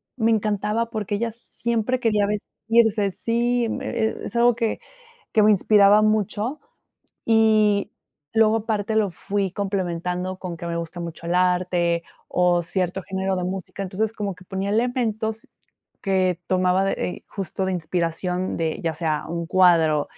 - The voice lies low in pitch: No, high, 195 Hz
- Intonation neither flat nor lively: Yes, average, 3.5 semitones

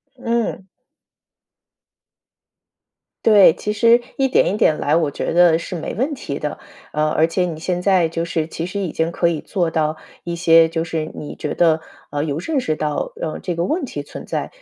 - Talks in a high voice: No, medium, 170 Hz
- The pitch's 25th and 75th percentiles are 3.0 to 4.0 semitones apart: Yes, average, 3.4 semitones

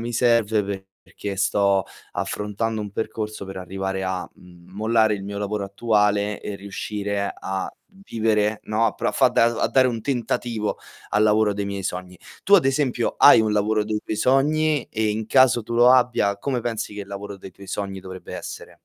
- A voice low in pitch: Yes, low, 105 Hz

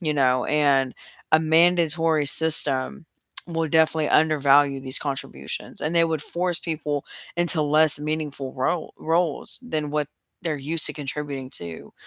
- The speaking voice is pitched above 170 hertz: No, medium, 150 Hz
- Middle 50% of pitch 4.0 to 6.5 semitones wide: No, narrow, 2.5 semitones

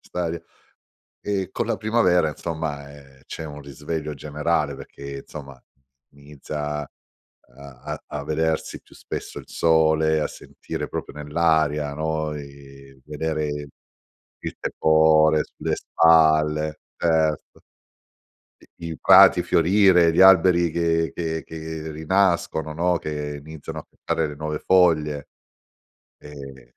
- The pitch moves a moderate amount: No, narrow, 2.0 semitones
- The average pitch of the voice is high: No, very low, 80 Hz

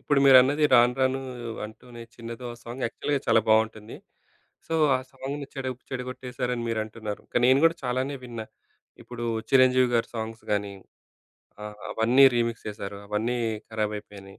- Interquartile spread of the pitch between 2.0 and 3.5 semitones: Yes, average, 2.8 semitones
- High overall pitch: No, low, 120 Hz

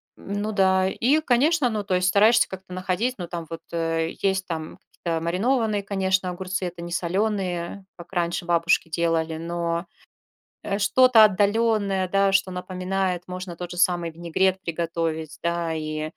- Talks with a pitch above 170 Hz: Yes, medium, 185 Hz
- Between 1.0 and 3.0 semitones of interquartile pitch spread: Yes, average, 2.7 semitones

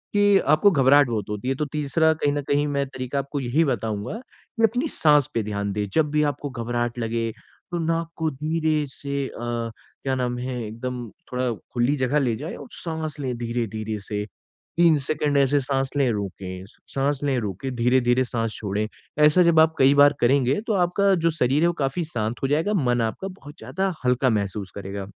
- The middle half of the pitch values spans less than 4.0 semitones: No, average, 4.4 semitones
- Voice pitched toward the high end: No, low, 135 Hz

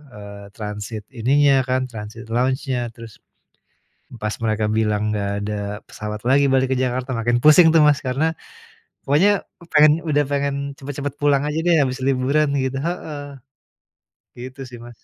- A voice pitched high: No, low, 130 Hz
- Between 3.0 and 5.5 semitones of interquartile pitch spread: Yes, average, 4.1 semitones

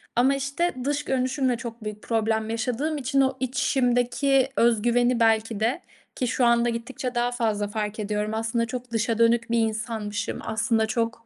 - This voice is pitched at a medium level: No, high, 235 Hz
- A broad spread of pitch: No, narrow, 2.4 semitones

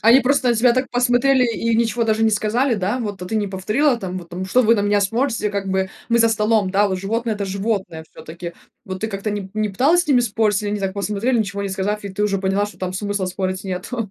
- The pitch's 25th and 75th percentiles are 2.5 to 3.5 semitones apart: Yes, average, 3.2 semitones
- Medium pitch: No, high, 210 Hz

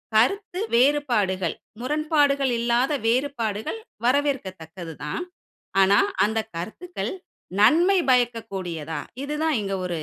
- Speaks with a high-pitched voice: Yes, high, 240 Hz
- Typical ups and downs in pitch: No, wide, 7.0 semitones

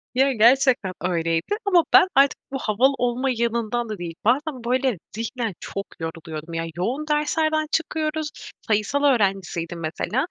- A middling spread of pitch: No, wide, 6.5 semitones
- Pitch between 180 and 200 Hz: No, high, 240 Hz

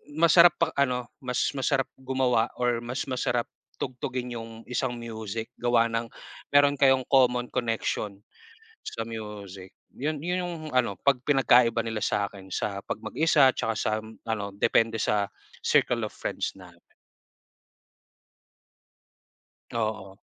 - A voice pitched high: No, low, 120 Hz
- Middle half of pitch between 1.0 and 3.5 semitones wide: Yes, average, 3.0 semitones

